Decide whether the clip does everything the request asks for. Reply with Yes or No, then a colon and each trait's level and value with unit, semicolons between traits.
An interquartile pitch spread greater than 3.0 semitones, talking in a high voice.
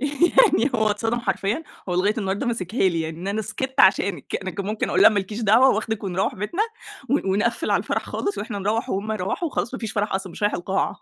Yes: average, 3.7 semitones; high, 210 Hz